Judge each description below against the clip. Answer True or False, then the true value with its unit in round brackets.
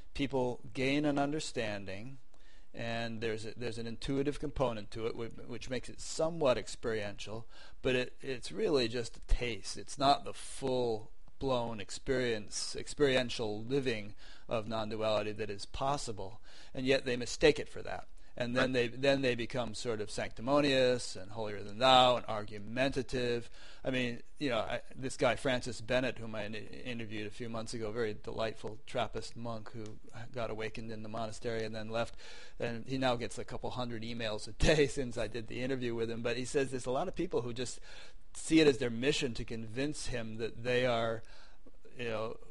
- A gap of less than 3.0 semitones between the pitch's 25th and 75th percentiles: True (2.6 semitones)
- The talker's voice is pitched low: True (120 Hz)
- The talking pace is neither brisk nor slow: True (185 wpm)